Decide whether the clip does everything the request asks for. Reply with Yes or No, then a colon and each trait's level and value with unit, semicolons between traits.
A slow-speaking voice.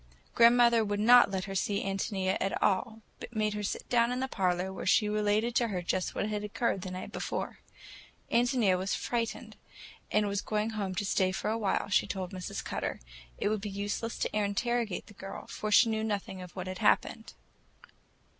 No: average, 200 wpm